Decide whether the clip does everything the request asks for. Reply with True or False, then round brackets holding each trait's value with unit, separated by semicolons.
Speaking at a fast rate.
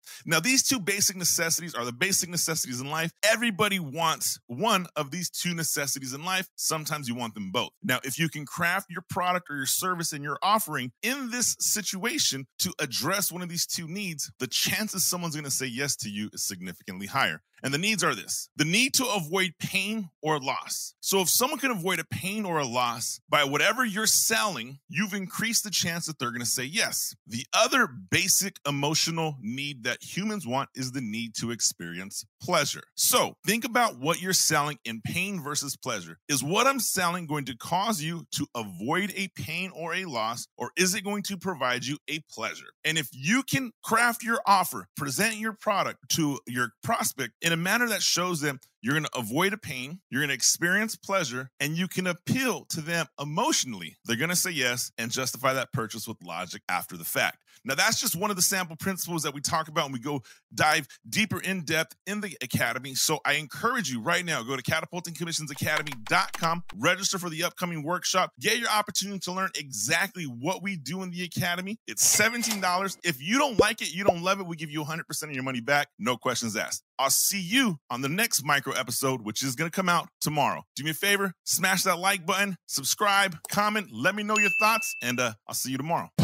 True (210 wpm)